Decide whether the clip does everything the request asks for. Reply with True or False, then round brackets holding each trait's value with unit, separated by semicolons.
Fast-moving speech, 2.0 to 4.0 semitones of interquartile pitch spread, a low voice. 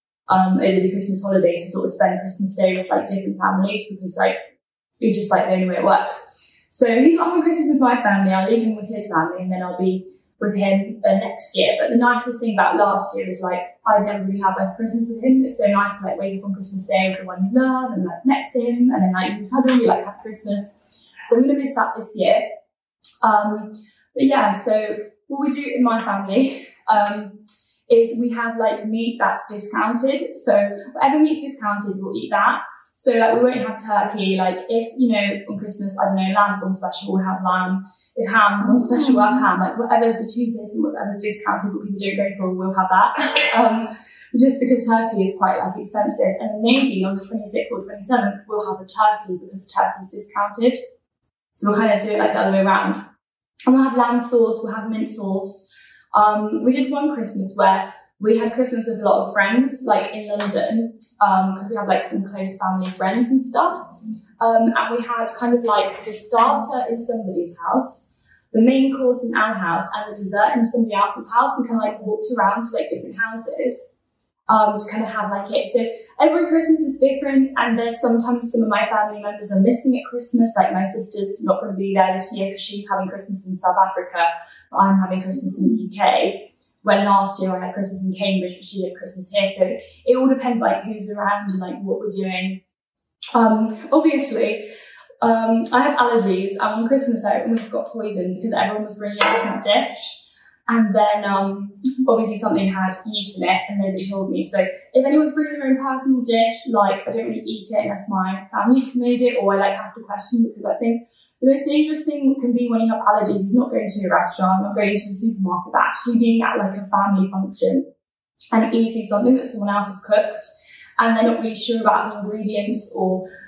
False (220 wpm; 3.6 semitones; 215 Hz)